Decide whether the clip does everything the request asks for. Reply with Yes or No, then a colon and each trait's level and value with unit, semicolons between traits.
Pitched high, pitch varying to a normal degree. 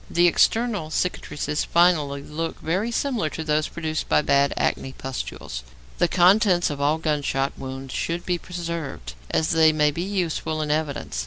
No: medium, 160 Hz; average, 3.2 semitones